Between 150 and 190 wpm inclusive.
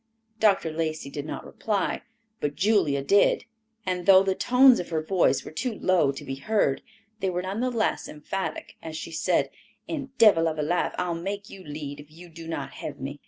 No: fast, 205 wpm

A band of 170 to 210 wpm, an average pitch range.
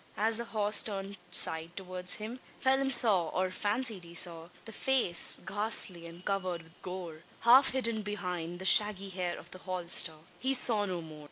Yes: average, 175 wpm; average, 3.9 semitones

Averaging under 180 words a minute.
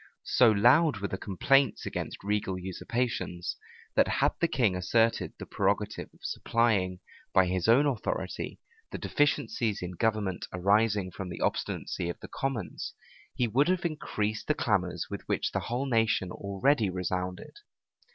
Yes: average, 150 wpm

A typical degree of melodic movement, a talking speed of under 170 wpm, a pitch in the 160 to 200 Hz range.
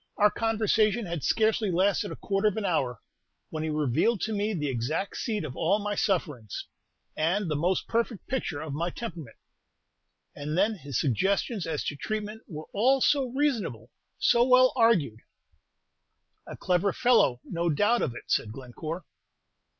No: wide, 6.4 semitones; average, 160 wpm; high, 190 Hz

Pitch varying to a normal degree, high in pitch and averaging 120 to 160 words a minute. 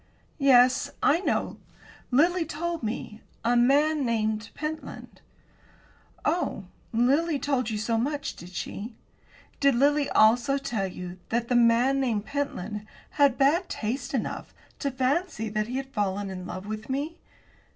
Yes: average, 4.7 semitones; very high, 250 Hz; average, 140 wpm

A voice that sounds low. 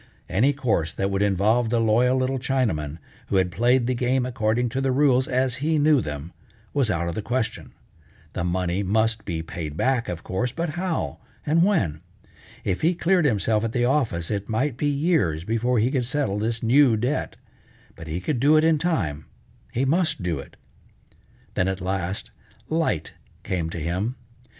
Yes: low, 115 Hz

